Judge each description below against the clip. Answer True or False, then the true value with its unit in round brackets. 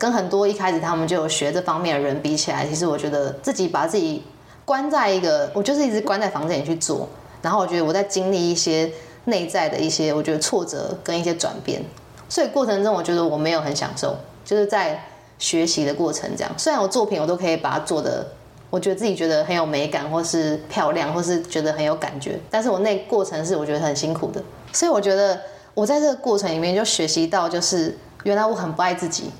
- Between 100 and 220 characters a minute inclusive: False (350 characters per minute)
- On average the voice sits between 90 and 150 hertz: False (175 Hz)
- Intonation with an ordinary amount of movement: True (4.3 semitones)